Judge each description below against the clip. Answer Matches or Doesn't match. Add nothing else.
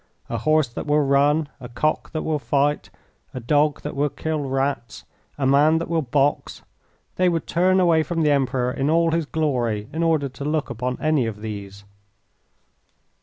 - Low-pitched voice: Doesn't match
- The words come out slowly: Doesn't match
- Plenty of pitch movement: Doesn't match